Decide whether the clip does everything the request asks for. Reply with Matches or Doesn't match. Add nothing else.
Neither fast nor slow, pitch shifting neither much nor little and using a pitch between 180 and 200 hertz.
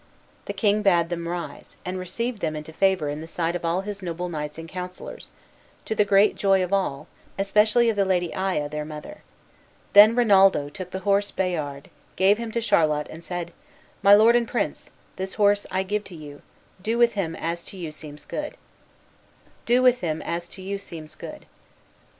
Matches